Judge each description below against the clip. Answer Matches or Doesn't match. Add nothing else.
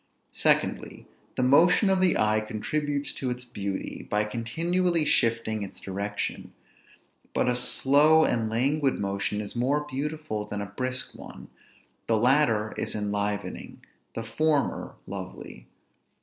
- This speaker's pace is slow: Matches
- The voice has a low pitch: Matches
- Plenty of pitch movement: Matches